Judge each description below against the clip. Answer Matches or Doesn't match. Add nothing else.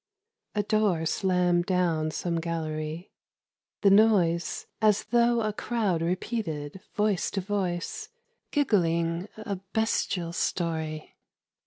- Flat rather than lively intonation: Doesn't match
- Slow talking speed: Matches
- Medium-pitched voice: Matches